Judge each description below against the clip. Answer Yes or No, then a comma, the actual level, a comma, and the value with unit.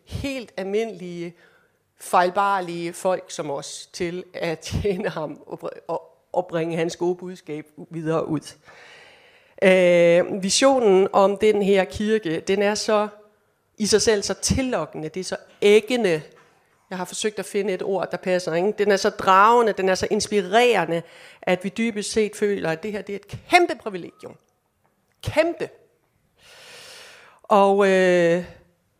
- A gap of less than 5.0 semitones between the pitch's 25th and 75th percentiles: Yes, average, 3.3 semitones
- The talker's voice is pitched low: No, high, 195 Hz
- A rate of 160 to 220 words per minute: No, slow, 145 wpm